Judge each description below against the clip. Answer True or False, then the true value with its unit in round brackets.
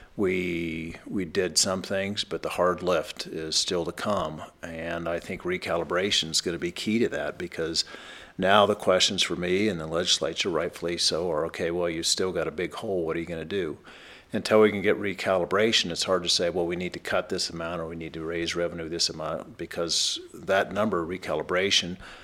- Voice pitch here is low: True (85 Hz)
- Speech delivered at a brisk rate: True (215 wpm)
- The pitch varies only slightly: True (1.6 semitones)